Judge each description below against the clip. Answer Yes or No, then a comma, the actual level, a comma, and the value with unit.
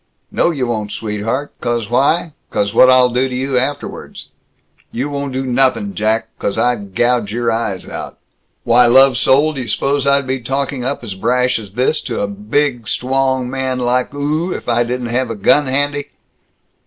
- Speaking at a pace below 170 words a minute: No, average, 180 wpm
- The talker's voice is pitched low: Yes, low, 125 Hz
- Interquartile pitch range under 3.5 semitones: Yes, average, 2.8 semitones